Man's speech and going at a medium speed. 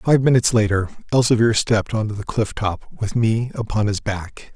Yes: male; average, 195 wpm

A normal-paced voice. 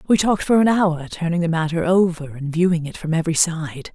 No: fast, 230 wpm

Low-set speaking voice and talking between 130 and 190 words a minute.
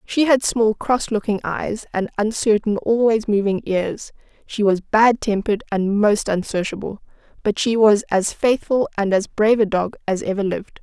No: high, 210 Hz; average, 170 wpm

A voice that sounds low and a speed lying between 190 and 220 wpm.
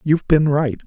No: medium, 150 Hz; fast, 210 wpm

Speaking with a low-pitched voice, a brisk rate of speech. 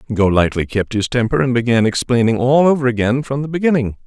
No: low, 125 Hz; average, 190 wpm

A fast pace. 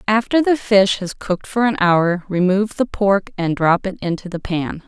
Yes: fast, 210 wpm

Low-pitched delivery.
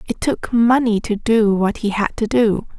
No: high, 220 Hz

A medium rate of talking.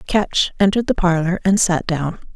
Yes: average, 180 wpm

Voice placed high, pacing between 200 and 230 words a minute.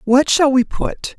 Yes: very high, 270 Hz; fast, 205 wpm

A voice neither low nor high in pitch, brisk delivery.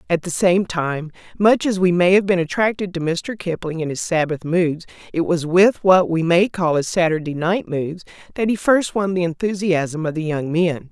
Yes: medium, 175 Hz; fast, 215 wpm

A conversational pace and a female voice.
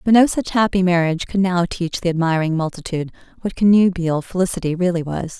Yes: average, 180 wpm; female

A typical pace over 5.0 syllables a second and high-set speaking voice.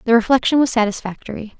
Yes: 7.0 syllables/s; high, 230 Hz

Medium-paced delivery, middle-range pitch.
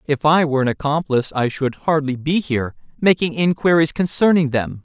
Yes: average, 160 wpm; medium, 150 Hz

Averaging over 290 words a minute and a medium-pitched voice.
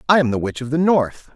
Yes: fast, 310 wpm; medium, 145 Hz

